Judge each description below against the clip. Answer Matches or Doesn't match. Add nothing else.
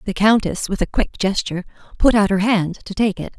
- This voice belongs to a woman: Matches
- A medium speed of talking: Doesn't match